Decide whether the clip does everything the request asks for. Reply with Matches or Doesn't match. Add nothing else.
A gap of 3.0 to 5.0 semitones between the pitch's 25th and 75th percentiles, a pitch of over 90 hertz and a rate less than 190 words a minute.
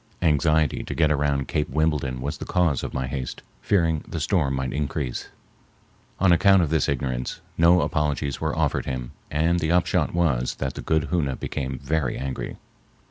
Doesn't match